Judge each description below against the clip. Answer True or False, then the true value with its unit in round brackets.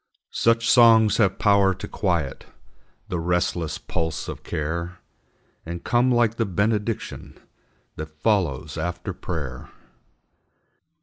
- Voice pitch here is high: False (90 Hz)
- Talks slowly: True (110 wpm)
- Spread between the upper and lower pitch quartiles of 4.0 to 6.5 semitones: True (5.2 semitones)